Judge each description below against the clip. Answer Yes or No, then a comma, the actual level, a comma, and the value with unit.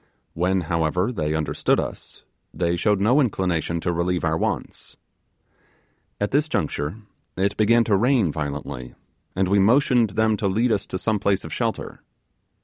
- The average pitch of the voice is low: Yes, very low, 95 Hz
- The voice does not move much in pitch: No, average, 4.8 semitones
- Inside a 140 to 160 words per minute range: Yes, average, 155 wpm